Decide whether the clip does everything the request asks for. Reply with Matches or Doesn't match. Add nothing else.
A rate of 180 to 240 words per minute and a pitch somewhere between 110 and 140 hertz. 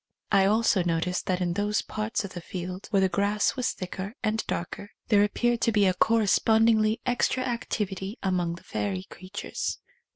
Doesn't match